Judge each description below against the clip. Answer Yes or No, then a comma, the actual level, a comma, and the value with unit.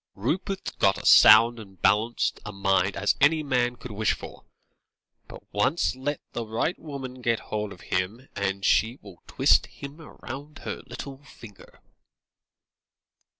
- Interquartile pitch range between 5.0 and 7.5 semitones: Yes, average, 5.3 semitones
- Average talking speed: Yes, average, 150 wpm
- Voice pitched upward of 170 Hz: No, low, 115 Hz